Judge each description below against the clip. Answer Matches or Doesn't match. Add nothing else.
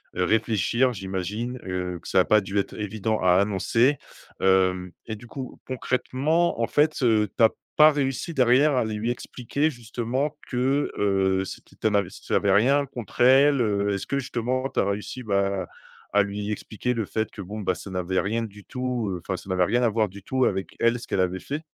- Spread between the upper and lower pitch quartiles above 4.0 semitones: Matches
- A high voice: Doesn't match